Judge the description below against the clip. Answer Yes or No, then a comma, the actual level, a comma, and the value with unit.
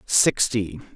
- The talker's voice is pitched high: No, low, 105 Hz